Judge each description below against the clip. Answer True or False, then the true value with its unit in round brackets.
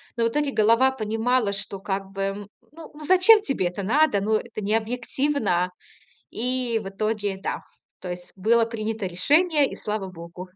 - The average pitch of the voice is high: True (220 Hz)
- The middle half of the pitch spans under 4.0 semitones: False (4.7 semitones)